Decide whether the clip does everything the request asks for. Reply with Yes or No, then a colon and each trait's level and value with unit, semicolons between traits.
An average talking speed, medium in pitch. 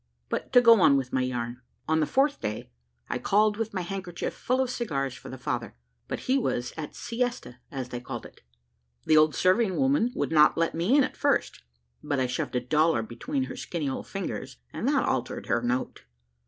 No: fast, 210 wpm; medium, 160 Hz